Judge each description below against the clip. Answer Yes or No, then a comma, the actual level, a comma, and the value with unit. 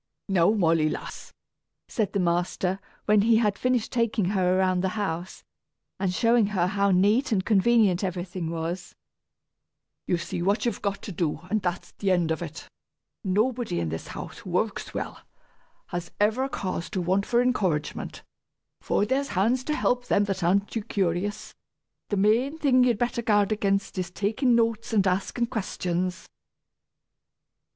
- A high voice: Yes, high, 200 Hz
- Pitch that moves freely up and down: No, average, 3.9 semitones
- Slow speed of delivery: No, average, 160 wpm